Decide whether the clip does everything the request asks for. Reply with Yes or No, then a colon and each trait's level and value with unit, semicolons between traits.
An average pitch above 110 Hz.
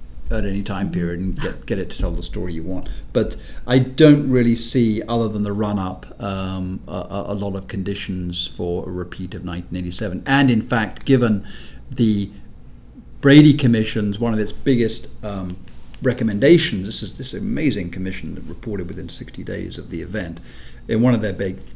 No: low, 100 Hz